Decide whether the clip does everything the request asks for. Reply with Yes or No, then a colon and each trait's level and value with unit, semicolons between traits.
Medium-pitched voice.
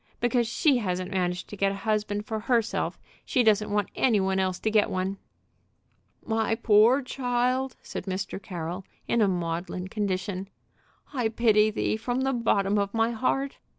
No: high, 210 Hz